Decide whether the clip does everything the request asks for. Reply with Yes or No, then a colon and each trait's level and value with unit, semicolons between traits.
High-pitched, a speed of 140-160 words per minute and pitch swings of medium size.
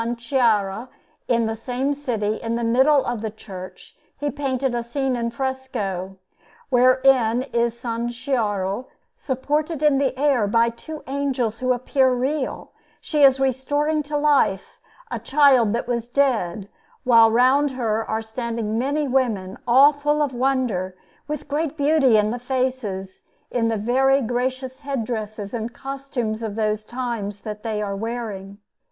Yes: high, 245 Hz; average, 155 wpm; average, 3.4 semitones